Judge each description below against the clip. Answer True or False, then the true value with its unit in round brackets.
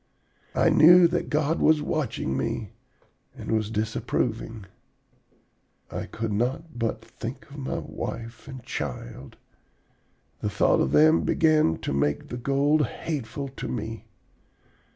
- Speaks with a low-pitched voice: True (120 Hz)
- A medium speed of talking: False (130 wpm)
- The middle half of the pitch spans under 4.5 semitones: False (5.6 semitones)